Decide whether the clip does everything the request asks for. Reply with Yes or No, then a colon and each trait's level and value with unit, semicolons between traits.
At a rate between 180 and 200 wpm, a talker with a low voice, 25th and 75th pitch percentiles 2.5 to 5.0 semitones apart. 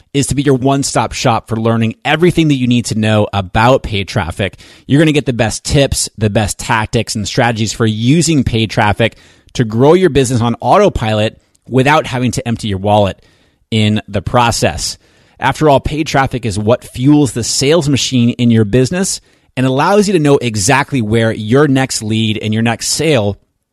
Yes: average, 190 wpm; low, 120 Hz; average, 4.0 semitones